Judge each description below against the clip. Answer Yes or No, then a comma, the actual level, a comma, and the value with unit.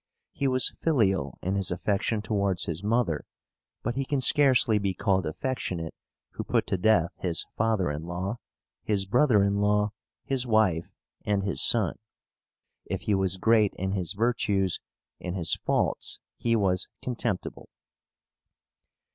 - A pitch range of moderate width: Yes, average, 3.7 semitones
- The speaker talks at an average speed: Yes, average, 145 wpm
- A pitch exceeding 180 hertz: No, low, 100 Hz